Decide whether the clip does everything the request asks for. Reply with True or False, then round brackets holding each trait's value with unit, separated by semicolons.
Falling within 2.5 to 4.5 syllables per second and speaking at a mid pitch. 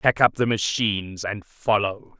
False (4.2 syllables/s; 105 Hz)